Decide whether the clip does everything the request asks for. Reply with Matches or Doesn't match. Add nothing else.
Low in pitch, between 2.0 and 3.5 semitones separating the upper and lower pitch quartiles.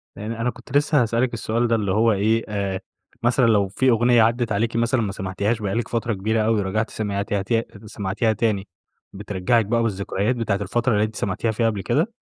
Matches